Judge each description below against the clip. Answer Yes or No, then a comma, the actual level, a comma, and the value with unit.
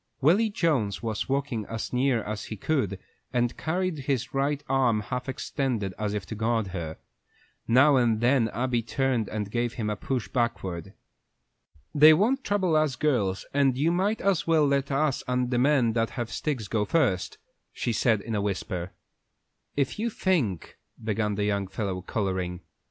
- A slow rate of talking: No, average, 175 wpm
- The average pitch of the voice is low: Yes, low, 120 Hz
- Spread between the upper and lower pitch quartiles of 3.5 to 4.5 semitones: No, average, 5.1 semitones